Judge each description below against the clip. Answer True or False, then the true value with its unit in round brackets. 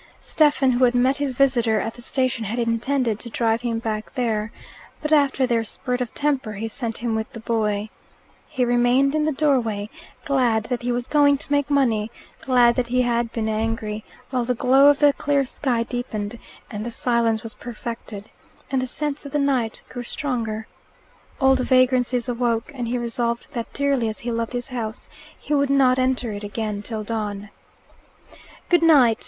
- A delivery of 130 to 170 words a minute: False (185 wpm)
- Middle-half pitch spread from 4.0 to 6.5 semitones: False (3.0 semitones)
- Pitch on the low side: False (240 Hz)